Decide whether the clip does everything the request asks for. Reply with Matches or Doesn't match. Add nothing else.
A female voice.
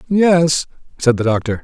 Doesn't match